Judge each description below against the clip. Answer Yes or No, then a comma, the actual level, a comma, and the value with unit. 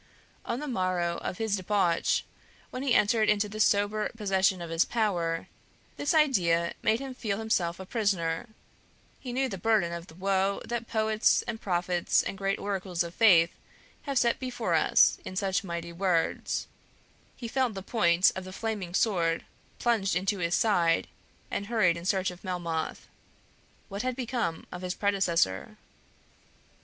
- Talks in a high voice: Yes, high, 195 Hz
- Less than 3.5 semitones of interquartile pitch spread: No, average, 4.2 semitones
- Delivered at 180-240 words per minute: No, average, 165 wpm